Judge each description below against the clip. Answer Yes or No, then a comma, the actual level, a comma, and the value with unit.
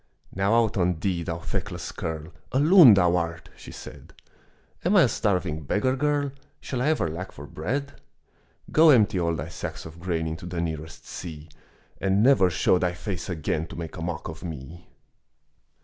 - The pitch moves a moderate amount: Yes, average, 4.4 semitones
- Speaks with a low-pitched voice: Yes, very low, 90 Hz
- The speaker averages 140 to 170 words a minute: No, average, 180 wpm